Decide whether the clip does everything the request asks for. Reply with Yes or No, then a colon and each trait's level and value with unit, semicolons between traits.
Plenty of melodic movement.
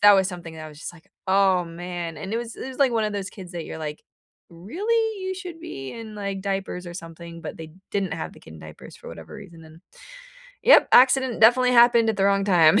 Yes: wide, 5.8 semitones